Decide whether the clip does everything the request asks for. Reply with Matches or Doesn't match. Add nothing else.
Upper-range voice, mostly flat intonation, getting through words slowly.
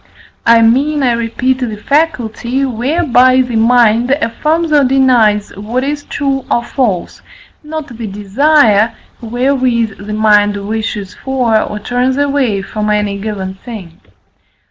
Doesn't match